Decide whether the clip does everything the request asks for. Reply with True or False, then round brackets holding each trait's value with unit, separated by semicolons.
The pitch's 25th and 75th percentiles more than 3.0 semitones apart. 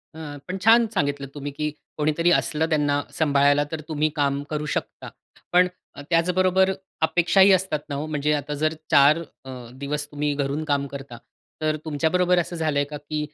False (2.5 semitones)